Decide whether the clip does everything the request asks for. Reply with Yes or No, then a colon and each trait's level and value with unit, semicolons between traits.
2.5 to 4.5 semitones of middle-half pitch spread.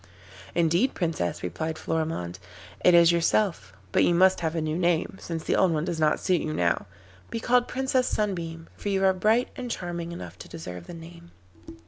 Yes: average, 2.9 semitones